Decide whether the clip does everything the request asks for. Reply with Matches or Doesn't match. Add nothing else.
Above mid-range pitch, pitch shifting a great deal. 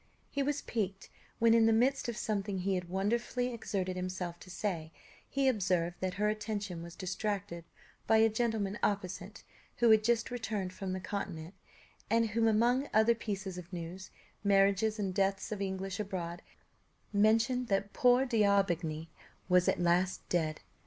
Doesn't match